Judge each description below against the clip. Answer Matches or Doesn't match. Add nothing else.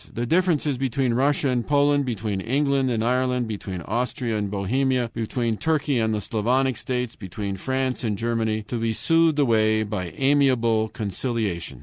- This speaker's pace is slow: Doesn't match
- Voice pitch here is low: Matches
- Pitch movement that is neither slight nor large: Matches